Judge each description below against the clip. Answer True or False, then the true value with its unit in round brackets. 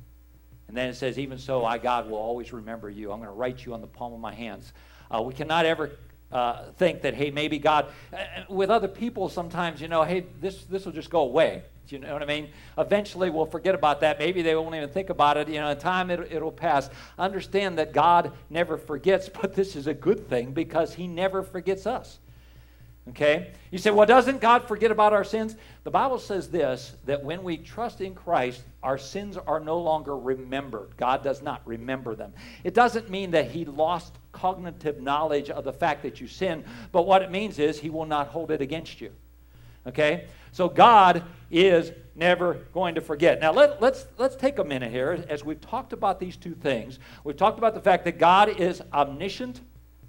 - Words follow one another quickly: True (210 wpm)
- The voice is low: False (155 Hz)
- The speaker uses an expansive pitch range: True (5.9 semitones)